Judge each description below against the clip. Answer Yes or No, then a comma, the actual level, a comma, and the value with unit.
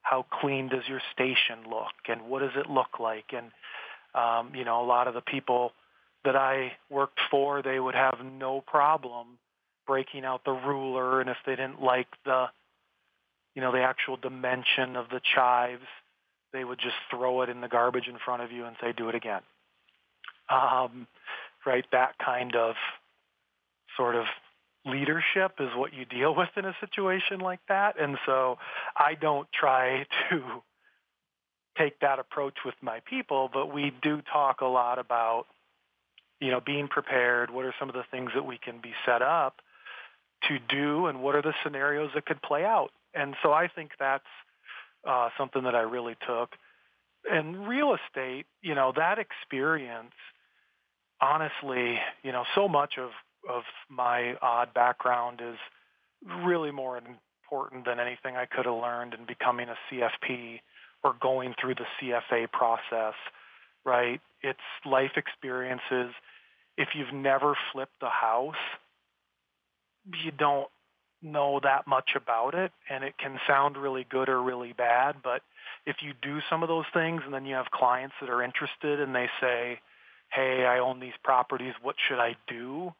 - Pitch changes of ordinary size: No, narrow, 2.3 semitones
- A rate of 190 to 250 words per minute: No, average, 165 wpm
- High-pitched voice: No, low, 130 Hz